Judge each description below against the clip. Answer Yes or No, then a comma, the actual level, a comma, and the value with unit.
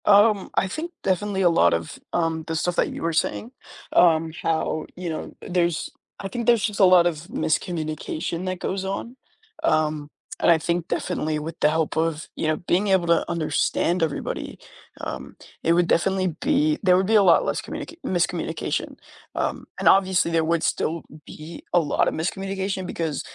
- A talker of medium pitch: Yes, medium, 175 Hz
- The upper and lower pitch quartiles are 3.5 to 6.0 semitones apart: No, average, 3.1 semitones